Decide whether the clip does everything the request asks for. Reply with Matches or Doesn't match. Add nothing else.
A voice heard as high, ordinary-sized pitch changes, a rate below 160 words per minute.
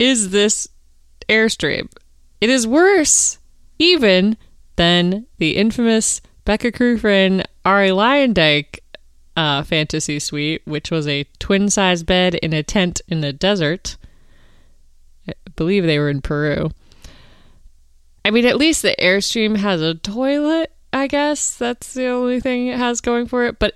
Doesn't match